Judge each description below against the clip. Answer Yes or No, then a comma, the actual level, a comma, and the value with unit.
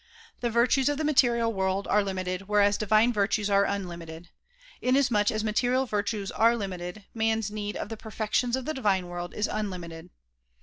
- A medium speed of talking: Yes, average, 170 wpm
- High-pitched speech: Yes, high, 210 Hz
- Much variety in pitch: No, average, 3.2 semitones